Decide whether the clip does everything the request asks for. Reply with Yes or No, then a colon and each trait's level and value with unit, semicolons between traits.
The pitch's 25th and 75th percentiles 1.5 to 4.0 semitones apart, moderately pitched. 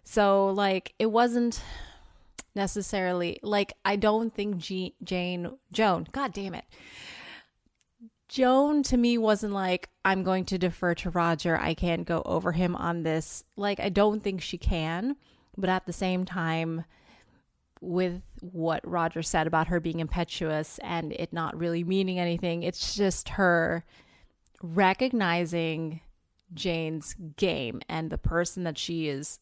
Yes: average, 3.1 semitones; medium, 180 Hz